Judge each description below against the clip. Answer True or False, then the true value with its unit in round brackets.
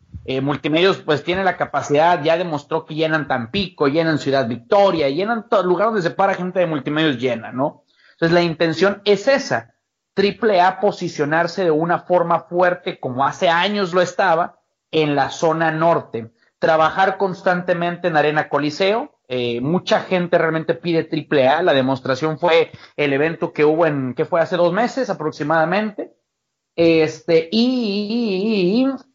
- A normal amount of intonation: True (3.9 semitones)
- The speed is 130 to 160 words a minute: True (155 wpm)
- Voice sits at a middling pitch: True (165 Hz)